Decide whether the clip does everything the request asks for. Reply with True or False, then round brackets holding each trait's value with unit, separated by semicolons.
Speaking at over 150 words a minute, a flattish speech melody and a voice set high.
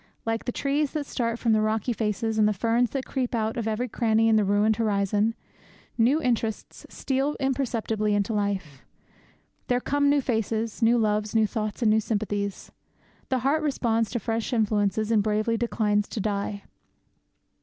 True (170 wpm; 2.3 semitones; 225 Hz)